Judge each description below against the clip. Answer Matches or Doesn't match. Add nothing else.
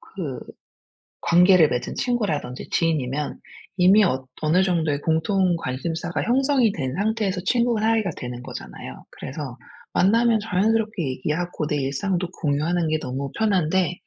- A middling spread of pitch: Doesn't match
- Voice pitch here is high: Doesn't match